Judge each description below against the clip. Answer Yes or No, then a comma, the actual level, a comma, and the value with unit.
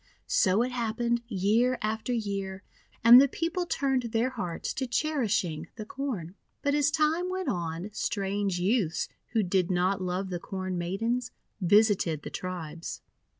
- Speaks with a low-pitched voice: No, high, 210 Hz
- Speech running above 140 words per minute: Yes, average, 150 wpm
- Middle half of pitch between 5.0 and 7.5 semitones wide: Yes, average, 5.3 semitones